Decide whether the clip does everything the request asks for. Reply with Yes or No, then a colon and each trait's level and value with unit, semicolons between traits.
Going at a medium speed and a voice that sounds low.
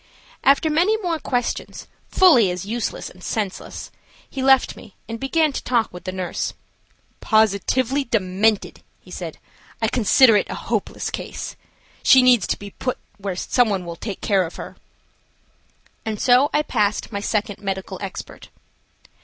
No: average, 155 wpm; high, 220 Hz